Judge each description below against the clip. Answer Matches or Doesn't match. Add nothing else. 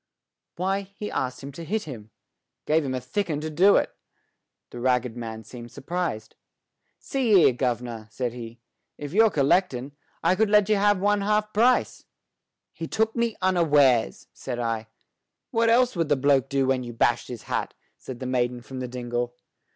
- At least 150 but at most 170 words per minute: Doesn't match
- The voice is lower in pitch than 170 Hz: Matches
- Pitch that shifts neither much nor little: Doesn't match